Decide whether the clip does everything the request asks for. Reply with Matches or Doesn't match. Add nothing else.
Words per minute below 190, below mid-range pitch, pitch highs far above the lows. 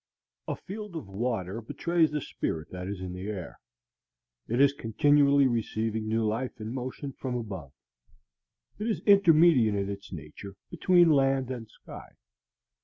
Matches